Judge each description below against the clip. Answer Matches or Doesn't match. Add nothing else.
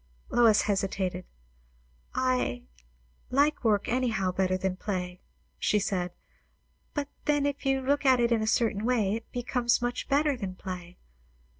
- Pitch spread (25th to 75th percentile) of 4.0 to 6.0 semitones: Matches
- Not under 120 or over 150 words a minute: Matches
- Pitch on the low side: Doesn't match